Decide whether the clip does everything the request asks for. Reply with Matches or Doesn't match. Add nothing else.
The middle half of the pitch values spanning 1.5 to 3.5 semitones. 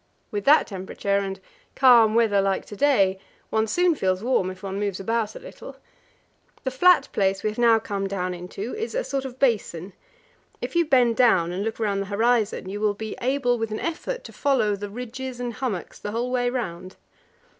Doesn't match